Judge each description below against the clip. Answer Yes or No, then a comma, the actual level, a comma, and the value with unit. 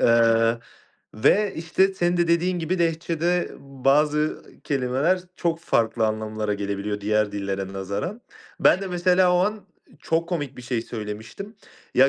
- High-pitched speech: No, medium, 145 Hz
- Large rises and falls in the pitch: Yes, wide, 8.2 semitones